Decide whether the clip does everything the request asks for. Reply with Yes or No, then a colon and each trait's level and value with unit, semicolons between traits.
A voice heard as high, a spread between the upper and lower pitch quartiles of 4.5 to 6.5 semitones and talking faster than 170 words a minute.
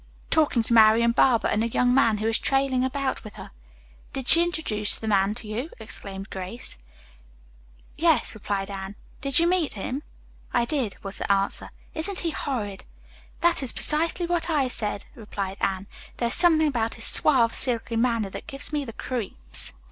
Yes: high, 235 Hz; average, 4.9 semitones; average, 180 wpm